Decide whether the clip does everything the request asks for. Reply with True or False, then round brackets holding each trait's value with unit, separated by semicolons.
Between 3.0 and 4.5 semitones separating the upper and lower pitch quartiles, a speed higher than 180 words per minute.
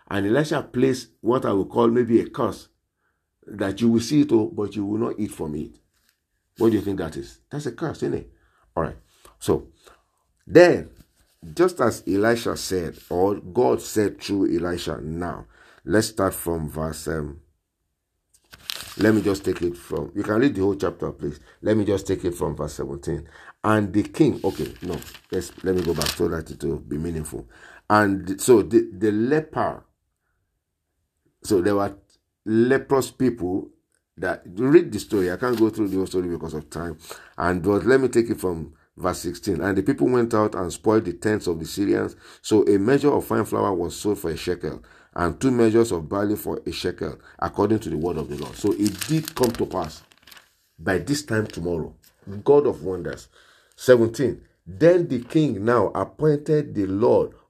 False (5.1 semitones; 190 wpm)